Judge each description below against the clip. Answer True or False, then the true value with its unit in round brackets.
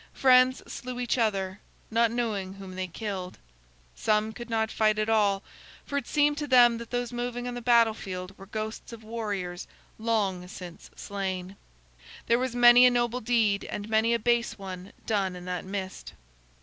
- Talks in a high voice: True (220 Hz)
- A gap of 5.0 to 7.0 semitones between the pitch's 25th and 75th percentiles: False (3.7 semitones)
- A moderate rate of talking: True (175 wpm)